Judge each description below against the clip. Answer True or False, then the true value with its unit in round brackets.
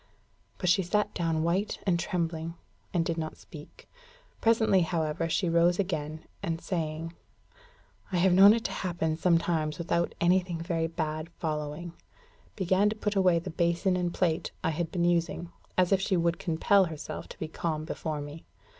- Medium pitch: True (170 Hz)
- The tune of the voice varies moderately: False (2.2 semitones)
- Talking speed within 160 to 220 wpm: True (165 wpm)